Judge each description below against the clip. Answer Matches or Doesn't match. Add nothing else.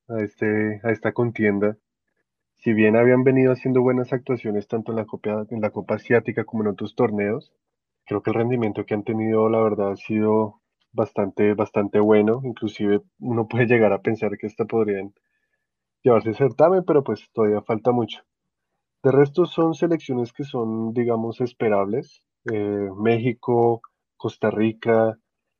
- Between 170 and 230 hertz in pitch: Doesn't match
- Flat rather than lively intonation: Matches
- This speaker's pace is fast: Doesn't match